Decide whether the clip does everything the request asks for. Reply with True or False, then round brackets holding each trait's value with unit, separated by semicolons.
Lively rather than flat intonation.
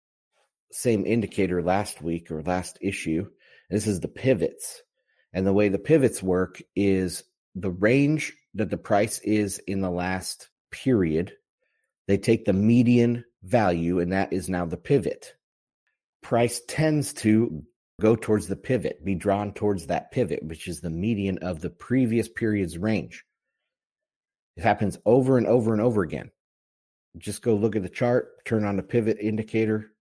False (3.9 semitones)